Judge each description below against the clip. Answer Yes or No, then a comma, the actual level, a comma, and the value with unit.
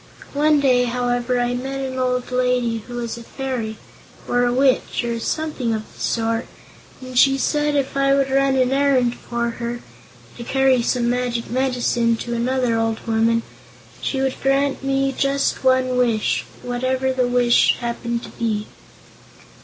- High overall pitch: Yes, very high, 250 Hz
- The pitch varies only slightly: Yes, narrow, 2.0 semitones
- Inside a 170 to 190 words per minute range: No, average, 160 wpm